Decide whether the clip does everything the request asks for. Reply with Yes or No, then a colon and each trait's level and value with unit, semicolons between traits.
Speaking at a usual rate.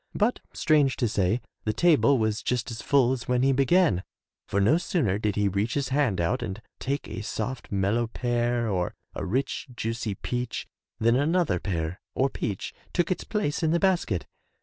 Yes: average, 185 wpm